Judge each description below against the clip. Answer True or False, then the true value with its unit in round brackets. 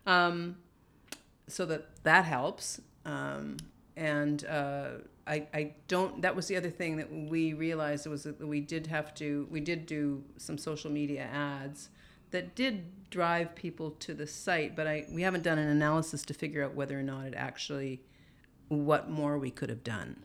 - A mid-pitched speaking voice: True (150 Hz)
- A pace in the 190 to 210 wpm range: False (180 wpm)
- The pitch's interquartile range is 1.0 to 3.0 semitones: True (2.4 semitones)